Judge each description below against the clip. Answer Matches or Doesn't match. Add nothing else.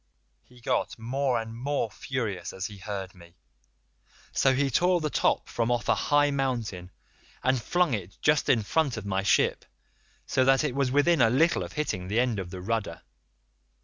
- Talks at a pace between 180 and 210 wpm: Matches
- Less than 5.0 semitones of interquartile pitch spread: Doesn't match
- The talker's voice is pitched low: Matches